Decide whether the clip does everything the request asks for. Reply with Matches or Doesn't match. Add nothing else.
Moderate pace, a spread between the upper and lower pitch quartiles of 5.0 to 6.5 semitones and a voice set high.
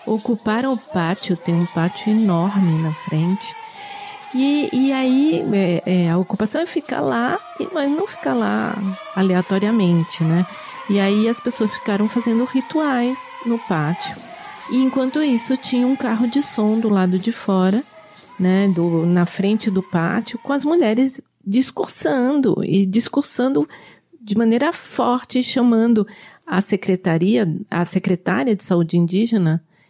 Matches